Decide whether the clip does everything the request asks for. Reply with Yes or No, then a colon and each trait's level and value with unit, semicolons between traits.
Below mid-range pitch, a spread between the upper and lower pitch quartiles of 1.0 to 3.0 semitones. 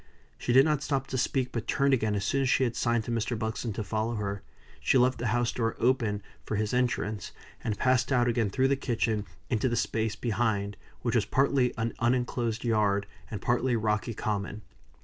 Yes: low, 115 Hz; average, 2.7 semitones